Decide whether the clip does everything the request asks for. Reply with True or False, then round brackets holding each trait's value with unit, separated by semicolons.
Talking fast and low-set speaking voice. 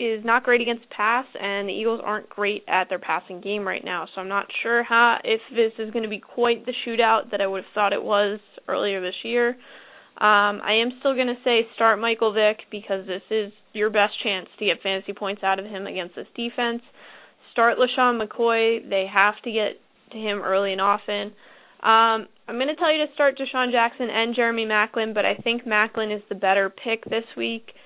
False (220 wpm; 220 Hz)